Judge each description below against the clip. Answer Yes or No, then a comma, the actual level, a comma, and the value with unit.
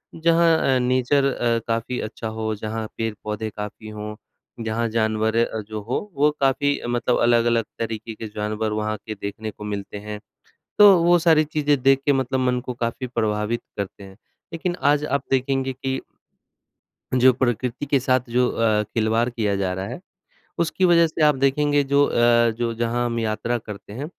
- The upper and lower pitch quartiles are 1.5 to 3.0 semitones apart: No, average, 3.7 semitones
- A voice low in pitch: Yes, low, 120 Hz